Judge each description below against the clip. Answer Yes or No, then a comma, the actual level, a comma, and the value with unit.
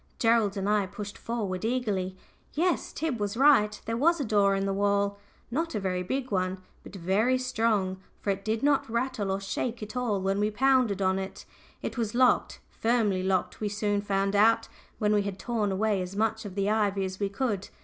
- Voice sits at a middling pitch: No, high, 210 Hz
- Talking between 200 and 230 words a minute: Yes, fast, 205 wpm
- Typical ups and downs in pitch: Yes, average, 3.0 semitones